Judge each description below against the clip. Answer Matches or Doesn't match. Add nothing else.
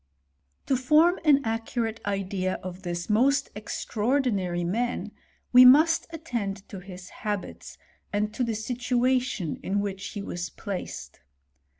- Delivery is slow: Matches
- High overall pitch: Matches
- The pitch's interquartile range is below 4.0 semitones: Doesn't match